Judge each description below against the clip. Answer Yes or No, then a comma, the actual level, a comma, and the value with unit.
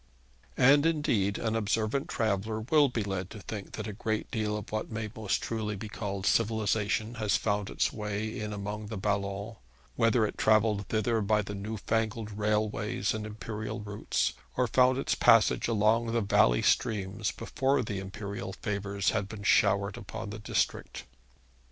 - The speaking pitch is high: No, low, 105 Hz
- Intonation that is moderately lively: No, narrow, 1.7 semitones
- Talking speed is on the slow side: No, average, 165 wpm